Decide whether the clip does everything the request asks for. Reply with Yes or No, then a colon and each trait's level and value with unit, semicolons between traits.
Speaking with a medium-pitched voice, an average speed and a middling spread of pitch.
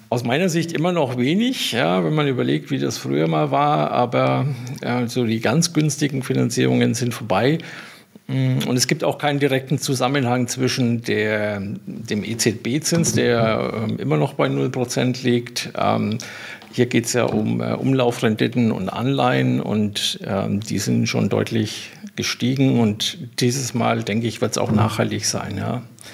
No: low, 120 Hz; average, 150 wpm; average, 3.6 semitones